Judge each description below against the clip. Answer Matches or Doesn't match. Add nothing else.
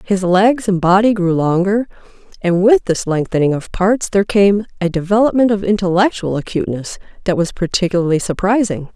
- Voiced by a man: Doesn't match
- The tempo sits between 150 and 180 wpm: Matches